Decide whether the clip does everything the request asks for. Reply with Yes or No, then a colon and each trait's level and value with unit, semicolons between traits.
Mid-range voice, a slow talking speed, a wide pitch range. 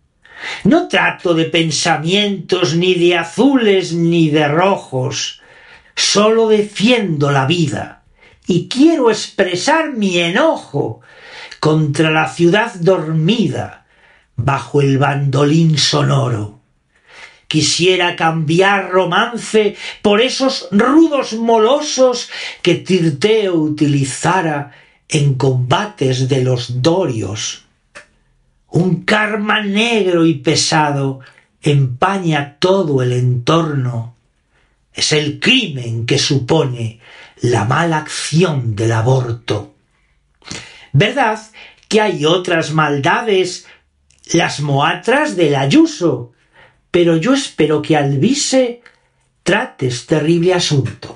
Yes: medium, 165 Hz; slow, 95 wpm; wide, 6.4 semitones